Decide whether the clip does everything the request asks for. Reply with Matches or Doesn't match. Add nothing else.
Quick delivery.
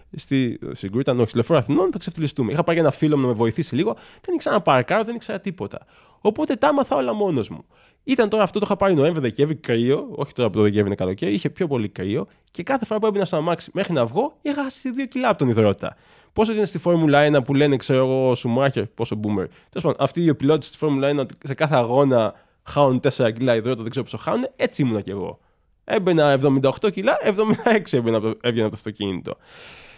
Matches